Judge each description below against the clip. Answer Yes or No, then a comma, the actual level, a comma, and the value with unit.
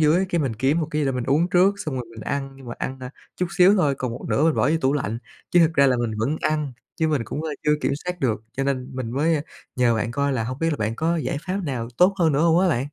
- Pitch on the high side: No, medium, 140 Hz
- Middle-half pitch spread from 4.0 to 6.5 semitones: Yes, average, 4.3 semitones